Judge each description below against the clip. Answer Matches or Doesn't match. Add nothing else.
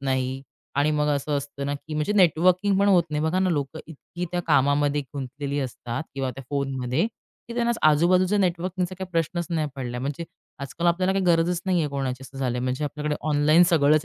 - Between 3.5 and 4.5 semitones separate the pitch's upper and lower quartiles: Matches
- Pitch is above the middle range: Doesn't match